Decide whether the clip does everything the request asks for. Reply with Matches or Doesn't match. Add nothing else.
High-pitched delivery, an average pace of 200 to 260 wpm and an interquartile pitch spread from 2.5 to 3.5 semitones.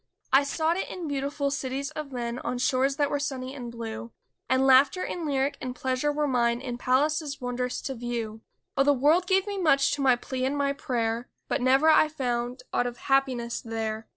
Matches